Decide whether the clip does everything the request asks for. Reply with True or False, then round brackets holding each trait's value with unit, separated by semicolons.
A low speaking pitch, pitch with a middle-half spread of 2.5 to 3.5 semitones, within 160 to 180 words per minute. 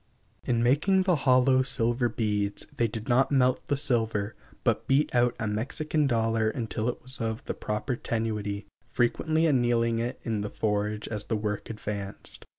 True (115 Hz; 3.2 semitones; 165 wpm)